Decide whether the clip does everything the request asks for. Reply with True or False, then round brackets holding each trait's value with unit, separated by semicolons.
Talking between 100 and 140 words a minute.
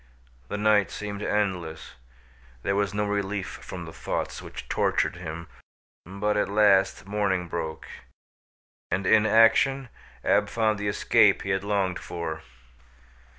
True (135 wpm)